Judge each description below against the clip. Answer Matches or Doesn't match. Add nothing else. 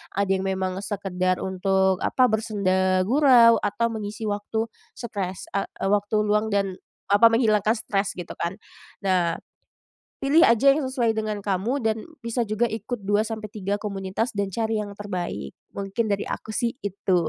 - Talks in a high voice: Matches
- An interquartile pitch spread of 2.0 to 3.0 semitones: Matches